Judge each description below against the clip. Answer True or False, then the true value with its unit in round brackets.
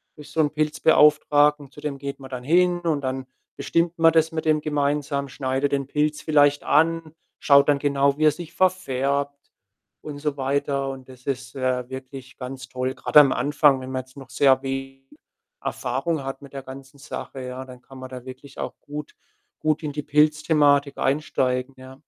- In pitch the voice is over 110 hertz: True (140 Hz)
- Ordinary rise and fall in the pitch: False (2.2 semitones)